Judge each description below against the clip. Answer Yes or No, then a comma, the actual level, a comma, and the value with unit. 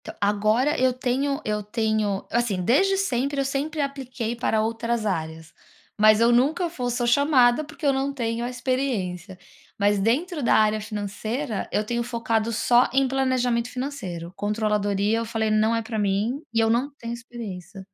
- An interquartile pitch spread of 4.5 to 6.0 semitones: No, average, 3.5 semitones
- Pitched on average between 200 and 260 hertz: Yes, high, 235 Hz